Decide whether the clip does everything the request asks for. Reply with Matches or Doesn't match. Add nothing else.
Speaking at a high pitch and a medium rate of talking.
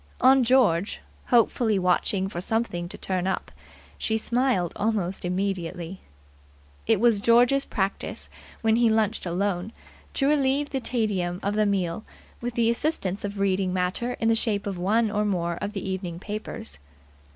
Matches